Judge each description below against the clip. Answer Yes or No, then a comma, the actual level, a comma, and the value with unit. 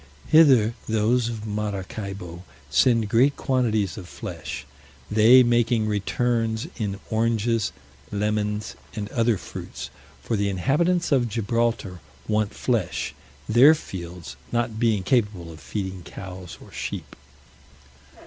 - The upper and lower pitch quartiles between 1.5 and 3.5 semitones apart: Yes, average, 3.1 semitones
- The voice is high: No, low, 110 Hz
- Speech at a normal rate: No, slow, 115 wpm